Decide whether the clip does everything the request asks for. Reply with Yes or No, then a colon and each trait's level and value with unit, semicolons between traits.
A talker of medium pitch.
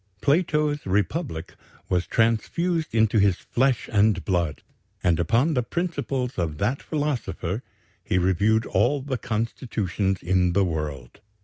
No: low, 110 Hz